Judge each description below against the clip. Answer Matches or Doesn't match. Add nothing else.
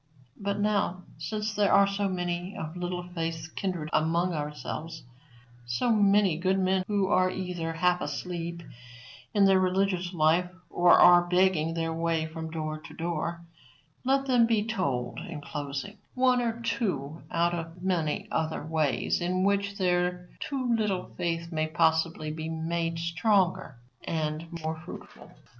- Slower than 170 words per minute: Matches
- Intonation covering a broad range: Doesn't match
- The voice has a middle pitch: Matches